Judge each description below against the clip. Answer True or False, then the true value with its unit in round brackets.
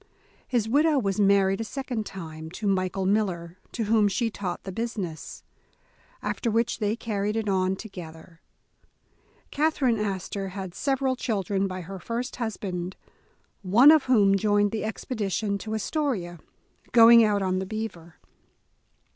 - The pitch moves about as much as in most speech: True (3.3 semitones)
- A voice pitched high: True (205 Hz)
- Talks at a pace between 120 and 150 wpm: True (140 wpm)